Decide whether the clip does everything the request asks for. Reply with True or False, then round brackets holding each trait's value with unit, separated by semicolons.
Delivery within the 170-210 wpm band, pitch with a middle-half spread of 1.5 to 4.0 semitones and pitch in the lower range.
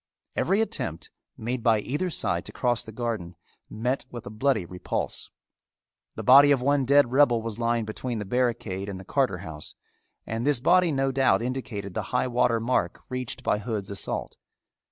True (175 wpm; 3.7 semitones; 120 Hz)